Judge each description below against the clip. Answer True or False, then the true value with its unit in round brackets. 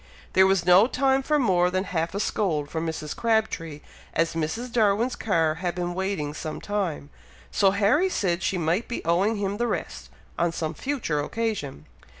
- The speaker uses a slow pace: False (175 wpm)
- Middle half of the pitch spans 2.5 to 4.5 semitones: False (5.0 semitones)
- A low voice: False (185 Hz)